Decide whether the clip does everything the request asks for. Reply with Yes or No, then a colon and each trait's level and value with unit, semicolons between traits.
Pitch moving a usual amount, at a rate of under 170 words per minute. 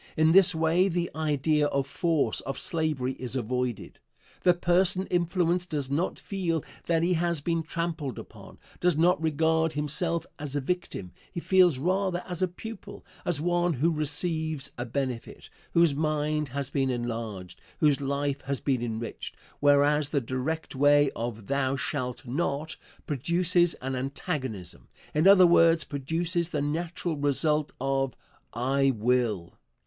Yes: average, 4.1 semitones; average, 145 wpm